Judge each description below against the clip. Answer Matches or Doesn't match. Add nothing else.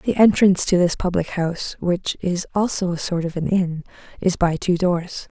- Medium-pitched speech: Matches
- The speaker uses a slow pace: Doesn't match